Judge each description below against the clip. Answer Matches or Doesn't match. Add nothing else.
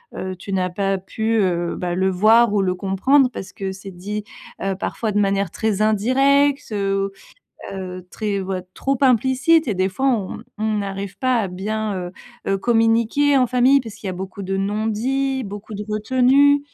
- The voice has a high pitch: Matches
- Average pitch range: Matches